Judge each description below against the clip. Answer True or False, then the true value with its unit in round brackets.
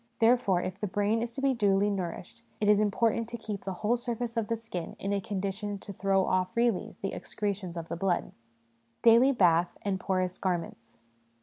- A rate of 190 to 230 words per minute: True (195 wpm)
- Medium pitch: False (200 Hz)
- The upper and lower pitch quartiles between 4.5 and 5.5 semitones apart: False (3.4 semitones)